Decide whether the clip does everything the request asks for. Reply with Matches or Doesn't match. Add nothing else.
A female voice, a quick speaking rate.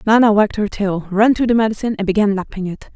Matches